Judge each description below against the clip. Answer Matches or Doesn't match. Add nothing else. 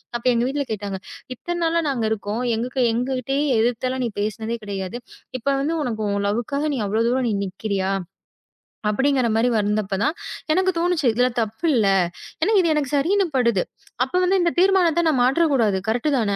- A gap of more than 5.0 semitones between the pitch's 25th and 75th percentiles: Matches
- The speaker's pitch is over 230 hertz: Matches